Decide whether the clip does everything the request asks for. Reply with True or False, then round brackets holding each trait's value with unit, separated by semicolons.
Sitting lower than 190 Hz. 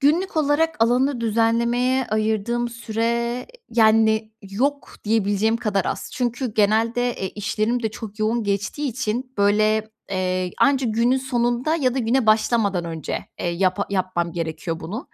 False (225 Hz)